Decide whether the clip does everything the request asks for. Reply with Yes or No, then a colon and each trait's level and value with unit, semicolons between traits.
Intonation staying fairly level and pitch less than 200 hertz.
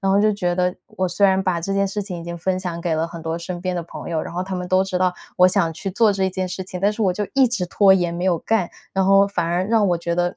Yes: narrow, 2.0 semitones; medium, 185 Hz